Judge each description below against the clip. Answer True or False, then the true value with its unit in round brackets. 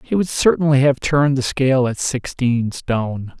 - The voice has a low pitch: True (130 Hz)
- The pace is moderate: True (175 wpm)